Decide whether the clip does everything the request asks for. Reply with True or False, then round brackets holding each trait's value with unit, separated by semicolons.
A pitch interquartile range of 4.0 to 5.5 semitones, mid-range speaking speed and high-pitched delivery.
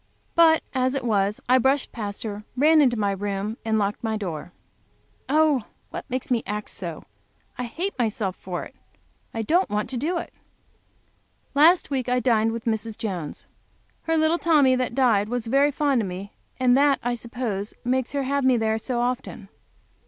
True (4.4 semitones; 175 wpm; 245 Hz)